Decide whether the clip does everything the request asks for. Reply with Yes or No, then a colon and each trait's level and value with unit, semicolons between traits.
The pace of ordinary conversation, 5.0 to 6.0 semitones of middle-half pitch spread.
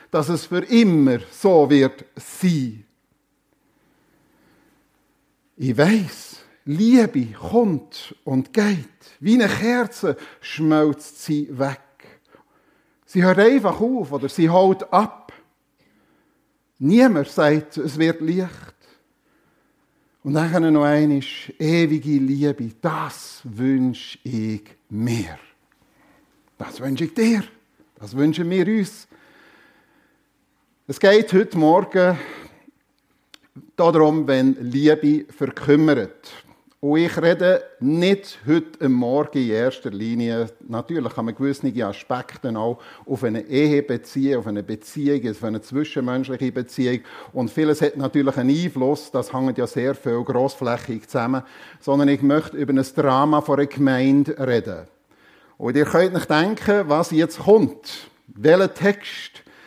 No: slow, 120 wpm; wide, 5.4 semitones